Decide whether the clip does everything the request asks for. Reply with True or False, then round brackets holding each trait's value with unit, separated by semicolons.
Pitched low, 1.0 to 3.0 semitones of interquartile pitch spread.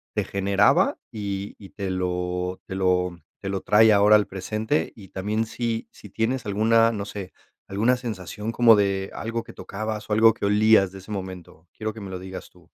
True (100 Hz; 2.6 semitones)